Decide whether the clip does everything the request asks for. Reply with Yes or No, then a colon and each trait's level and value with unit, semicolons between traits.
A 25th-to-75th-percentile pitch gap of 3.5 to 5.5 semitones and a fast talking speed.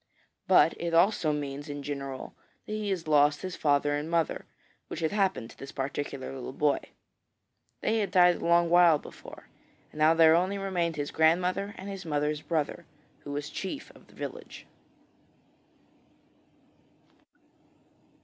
No: average, 3.8 semitones; average, 150 wpm